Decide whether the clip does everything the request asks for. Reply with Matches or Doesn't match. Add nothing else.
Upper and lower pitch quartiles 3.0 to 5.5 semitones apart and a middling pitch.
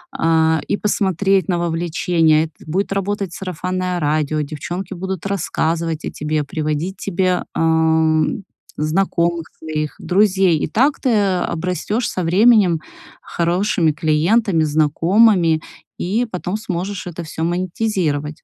Matches